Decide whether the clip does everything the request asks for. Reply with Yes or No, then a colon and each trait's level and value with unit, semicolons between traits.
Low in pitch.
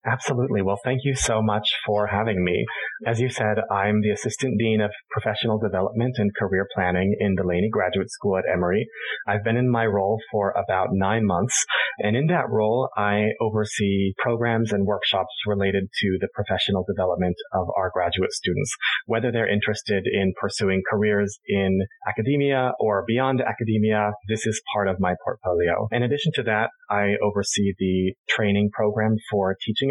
Yes: low, 105 Hz